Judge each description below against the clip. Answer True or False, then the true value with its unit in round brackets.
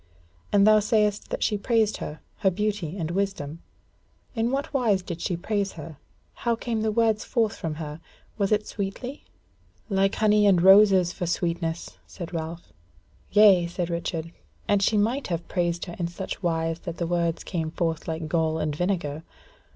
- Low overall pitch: False (185 Hz)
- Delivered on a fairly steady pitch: False (4.0 semitones)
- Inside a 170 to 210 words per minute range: True (175 wpm)